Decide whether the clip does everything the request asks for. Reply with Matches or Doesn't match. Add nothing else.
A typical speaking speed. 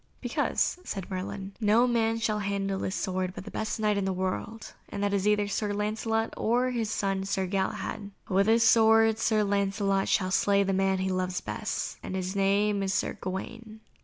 Matches